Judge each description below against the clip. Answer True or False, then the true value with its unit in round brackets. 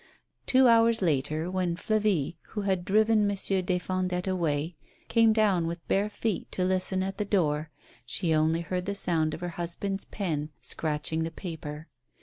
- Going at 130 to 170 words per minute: True (165 wpm)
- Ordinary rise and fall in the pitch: True (3.7 semitones)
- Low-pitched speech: False (180 Hz)